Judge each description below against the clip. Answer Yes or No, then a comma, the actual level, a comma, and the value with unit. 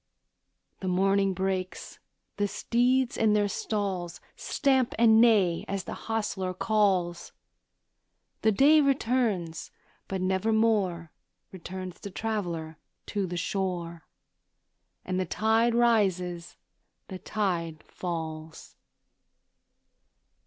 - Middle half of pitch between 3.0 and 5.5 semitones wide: Yes, average, 3.8 semitones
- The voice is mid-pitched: No, high, 195 Hz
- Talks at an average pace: No, slow, 95 wpm